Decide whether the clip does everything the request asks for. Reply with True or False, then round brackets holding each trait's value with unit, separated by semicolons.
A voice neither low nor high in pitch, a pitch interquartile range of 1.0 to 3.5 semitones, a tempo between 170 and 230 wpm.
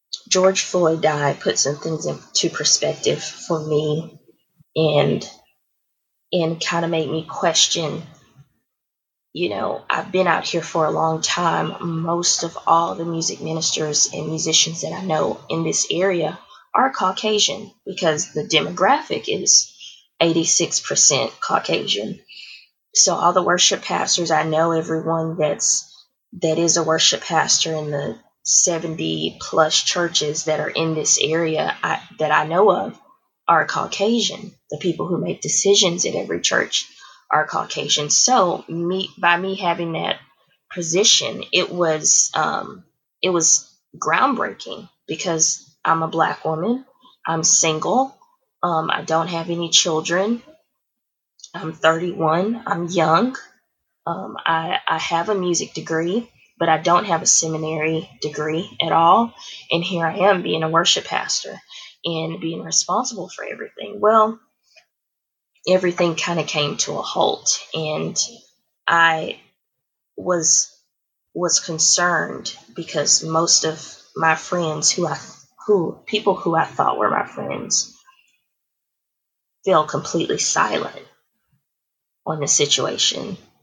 False (165 Hz; 2.7 semitones; 135 wpm)